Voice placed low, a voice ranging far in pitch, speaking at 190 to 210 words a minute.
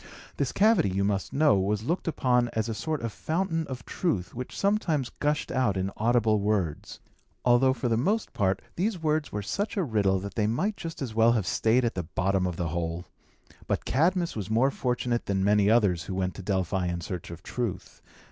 Yes: low, 115 Hz; wide, 6.4 semitones; fast, 205 wpm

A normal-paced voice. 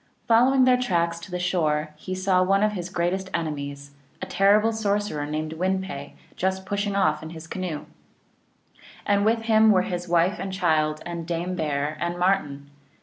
Yes: average, 175 wpm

